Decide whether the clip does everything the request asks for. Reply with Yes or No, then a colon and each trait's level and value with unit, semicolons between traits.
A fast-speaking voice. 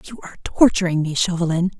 No: average, 165 wpm